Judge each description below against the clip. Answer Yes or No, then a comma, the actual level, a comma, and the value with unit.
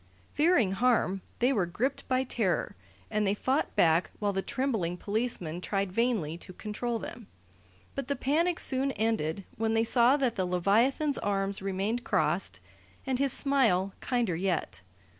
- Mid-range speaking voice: No, high, 220 Hz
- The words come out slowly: No, average, 155 wpm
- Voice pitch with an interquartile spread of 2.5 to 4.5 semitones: No, average, 5.2 semitones